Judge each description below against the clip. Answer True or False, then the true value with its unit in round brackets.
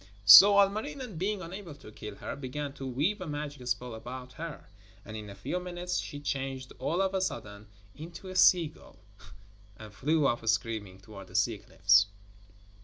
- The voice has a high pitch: False (140 Hz)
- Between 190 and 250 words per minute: False (175 wpm)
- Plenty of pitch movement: True (8.4 semitones)